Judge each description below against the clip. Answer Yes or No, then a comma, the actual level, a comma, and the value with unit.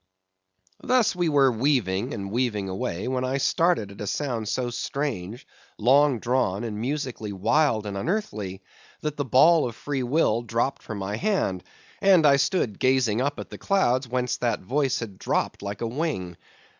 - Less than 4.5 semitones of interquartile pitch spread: No, wide, 5.5 semitones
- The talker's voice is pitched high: No, low, 125 Hz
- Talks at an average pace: Yes, average, 170 wpm